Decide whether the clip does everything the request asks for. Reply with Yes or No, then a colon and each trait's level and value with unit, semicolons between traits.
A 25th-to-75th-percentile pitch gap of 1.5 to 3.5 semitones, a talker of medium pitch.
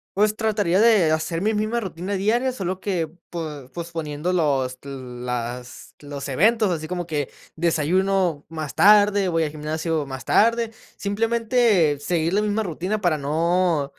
No: average, 5.3 semitones; medium, 170 Hz